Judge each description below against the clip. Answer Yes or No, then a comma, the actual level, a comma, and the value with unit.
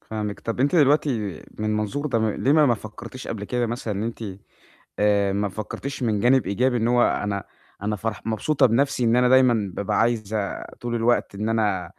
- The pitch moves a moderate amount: Yes, average, 3.0 semitones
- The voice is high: No, low, 115 Hz